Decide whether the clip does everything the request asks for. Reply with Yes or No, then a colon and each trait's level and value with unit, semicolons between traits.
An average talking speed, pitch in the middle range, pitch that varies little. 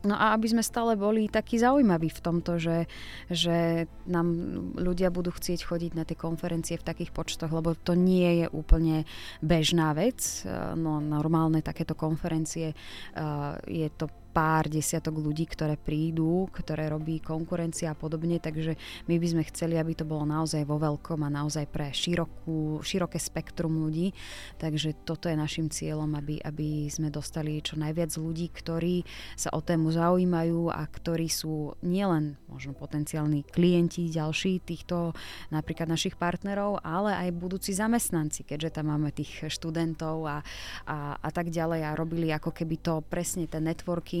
Yes: average, 155 wpm; medium, 160 Hz; narrow, 1.8 semitones